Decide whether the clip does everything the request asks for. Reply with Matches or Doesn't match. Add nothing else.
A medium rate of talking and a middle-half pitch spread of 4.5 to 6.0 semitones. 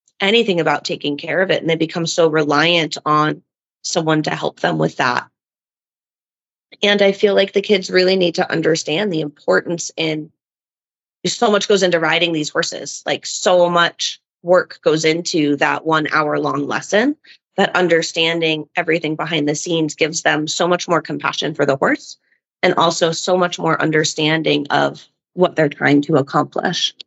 Doesn't match